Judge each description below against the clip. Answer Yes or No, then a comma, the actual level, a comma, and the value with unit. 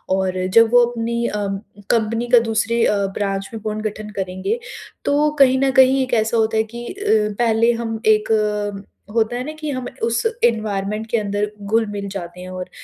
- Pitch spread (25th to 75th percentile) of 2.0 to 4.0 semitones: Yes, narrow, 2.6 semitones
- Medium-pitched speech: No, high, 220 Hz